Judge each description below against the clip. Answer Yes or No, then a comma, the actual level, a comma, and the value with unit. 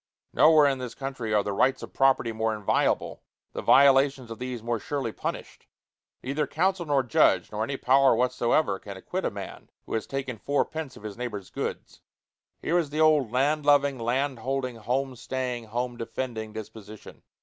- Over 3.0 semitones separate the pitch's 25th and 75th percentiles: Yes, average, 3.7 semitones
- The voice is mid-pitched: No, low, 130 Hz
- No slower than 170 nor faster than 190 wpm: Yes, average, 175 wpm